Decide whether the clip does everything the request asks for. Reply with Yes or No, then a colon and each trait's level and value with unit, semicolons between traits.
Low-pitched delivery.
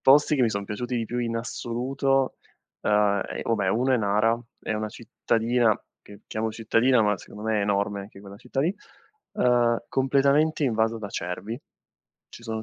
Yes: low, 115 Hz